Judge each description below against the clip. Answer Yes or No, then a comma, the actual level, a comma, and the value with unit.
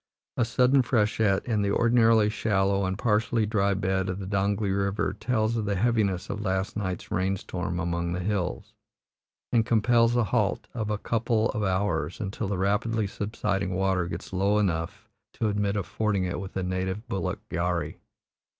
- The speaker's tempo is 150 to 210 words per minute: Yes, average, 170 wpm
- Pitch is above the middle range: No, low, 100 Hz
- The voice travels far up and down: No, average, 2.7 semitones